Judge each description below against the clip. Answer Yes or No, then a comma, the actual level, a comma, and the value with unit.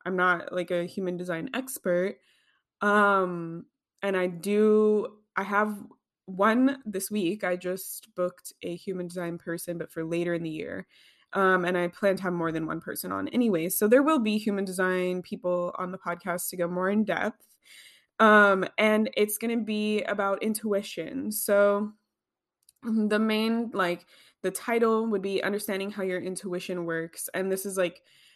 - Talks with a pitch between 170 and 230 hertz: Yes, high, 190 Hz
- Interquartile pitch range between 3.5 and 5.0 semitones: No, average, 3.0 semitones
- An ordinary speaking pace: Yes, average, 170 wpm